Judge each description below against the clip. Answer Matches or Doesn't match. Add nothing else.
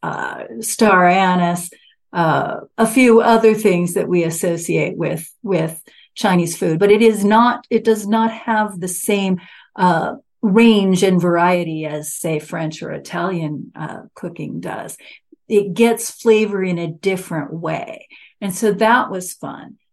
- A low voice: Doesn't match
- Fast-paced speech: Doesn't match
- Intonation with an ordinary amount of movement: Matches